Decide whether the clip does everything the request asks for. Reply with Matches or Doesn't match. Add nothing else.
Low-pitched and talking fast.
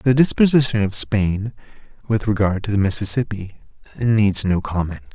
Doesn't match